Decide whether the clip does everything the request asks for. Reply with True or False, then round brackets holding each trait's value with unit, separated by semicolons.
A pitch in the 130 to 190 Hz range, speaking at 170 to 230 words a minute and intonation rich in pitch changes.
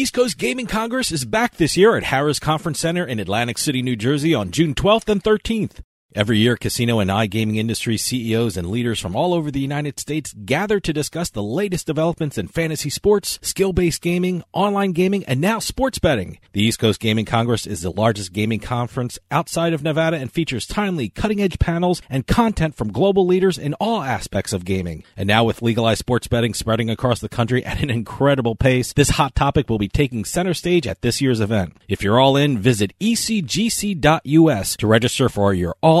True (140 Hz; 200 wpm; 7.6 semitones)